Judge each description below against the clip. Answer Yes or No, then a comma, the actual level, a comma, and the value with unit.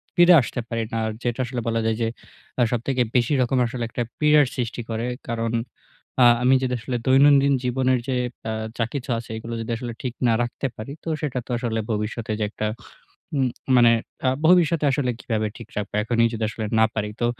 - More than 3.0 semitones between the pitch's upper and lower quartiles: No, narrow, 2.5 semitones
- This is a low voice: Yes, low, 120 Hz